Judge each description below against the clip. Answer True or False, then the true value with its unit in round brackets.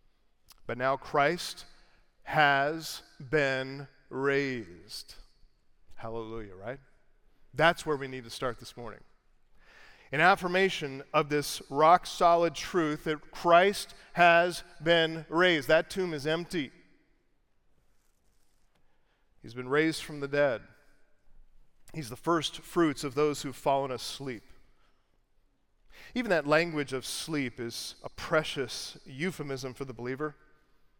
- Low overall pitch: False (150 Hz)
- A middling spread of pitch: True (3.7 semitones)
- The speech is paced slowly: True (115 wpm)